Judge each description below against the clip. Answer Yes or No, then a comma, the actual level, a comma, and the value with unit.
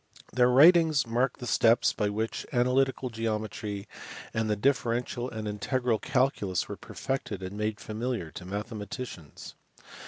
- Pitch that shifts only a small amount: No, average, 3.5 semitones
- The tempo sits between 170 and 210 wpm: No, slow, 135 wpm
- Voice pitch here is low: Yes, low, 115 Hz